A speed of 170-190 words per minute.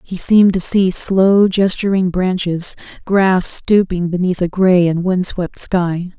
No: average, 155 wpm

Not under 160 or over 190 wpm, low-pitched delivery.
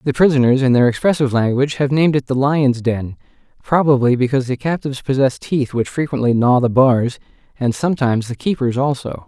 Yes: average, 180 wpm; low, 130 Hz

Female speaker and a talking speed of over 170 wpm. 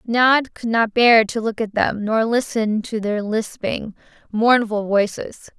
No: female; average, 160 wpm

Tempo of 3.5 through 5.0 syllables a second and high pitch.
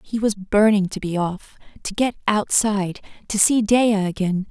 Yes: 4.6 syllables/s; high, 205 Hz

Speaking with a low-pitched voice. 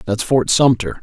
Yes: low, 115 Hz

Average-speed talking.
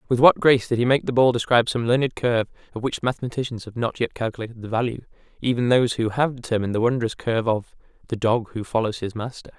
No: fast, 220 wpm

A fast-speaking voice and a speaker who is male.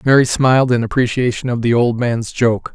No: average, 195 wpm; male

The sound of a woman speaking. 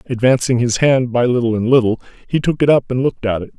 No: male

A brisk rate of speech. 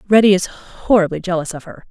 No: average, 190 wpm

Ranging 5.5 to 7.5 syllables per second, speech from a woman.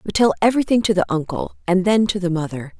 Yes: 6.5 syllables/s; female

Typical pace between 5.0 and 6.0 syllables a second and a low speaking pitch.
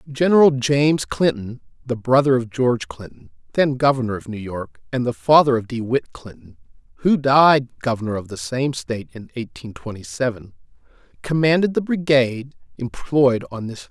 Yes: 5.2 syllables/s; low, 125 Hz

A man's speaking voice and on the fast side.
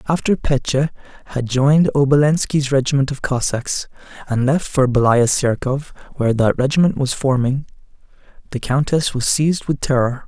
No: male; average, 140 wpm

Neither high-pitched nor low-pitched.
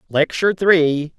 Yes: medium, 165 Hz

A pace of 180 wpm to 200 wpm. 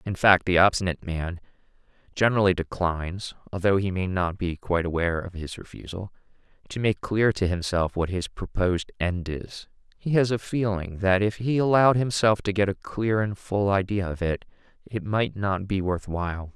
Yes: average, 185 wpm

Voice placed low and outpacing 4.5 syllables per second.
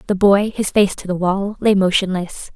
No: high, 195 Hz; 4.8 syllables/s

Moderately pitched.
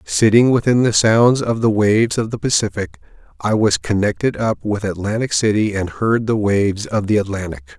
No: low, 110 Hz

